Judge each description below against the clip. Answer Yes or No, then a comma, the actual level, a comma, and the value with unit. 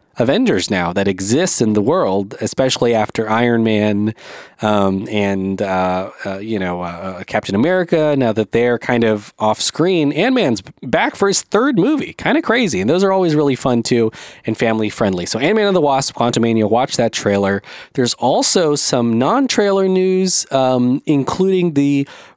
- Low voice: Yes, low, 115 Hz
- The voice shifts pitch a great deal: Yes, wide, 6.2 semitones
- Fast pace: No, average, 170 wpm